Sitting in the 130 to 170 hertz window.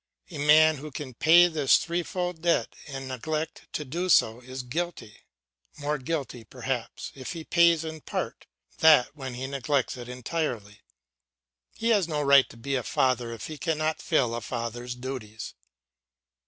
Yes: medium, 140 Hz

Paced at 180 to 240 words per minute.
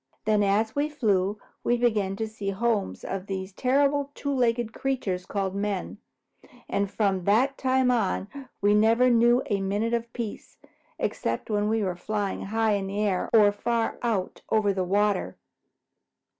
No: average, 165 wpm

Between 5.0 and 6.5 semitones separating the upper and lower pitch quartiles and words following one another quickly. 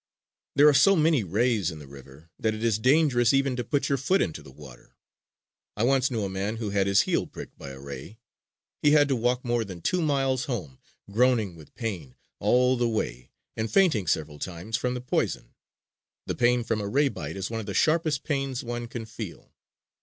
Yes: wide, 5.5 semitones; fast, 210 wpm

